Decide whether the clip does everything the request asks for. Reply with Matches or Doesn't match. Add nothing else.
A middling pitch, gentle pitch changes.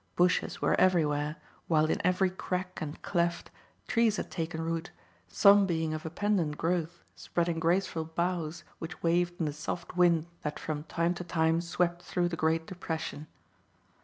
Matches